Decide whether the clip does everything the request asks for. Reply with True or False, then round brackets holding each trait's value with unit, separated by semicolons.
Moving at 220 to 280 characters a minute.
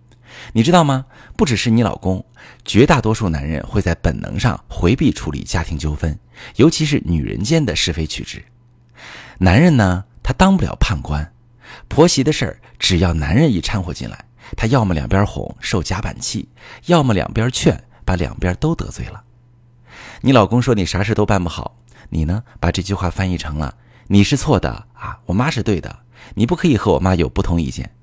True (275 characters per minute)